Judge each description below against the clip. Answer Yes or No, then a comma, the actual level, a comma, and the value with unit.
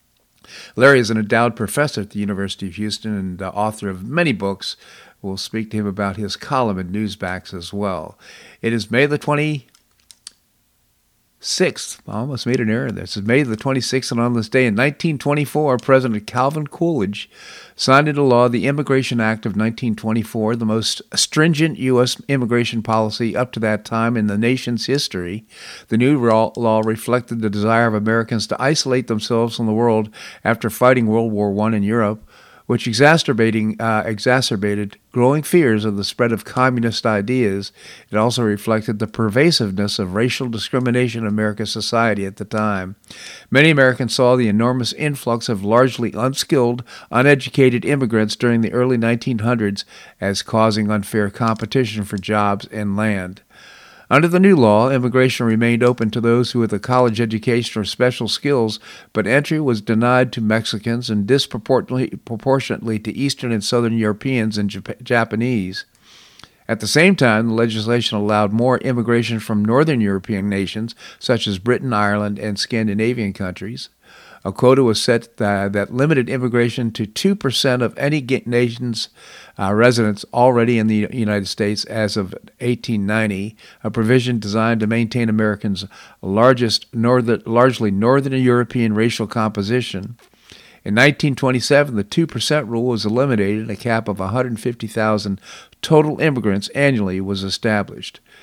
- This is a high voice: No, low, 115 Hz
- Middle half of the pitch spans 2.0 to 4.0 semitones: Yes, average, 2.9 semitones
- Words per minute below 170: Yes, average, 155 wpm